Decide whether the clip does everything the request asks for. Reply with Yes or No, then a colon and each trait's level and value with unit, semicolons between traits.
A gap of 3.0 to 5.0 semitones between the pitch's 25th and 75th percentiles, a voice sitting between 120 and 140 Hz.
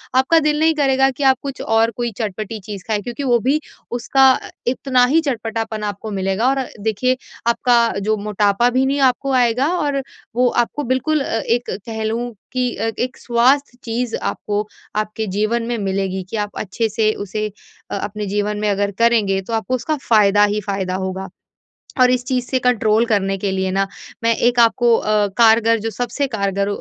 No: average, 3.4 semitones; high, 225 Hz